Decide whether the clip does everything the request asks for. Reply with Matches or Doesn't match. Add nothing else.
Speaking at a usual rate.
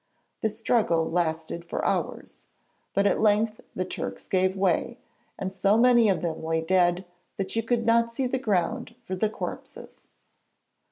Matches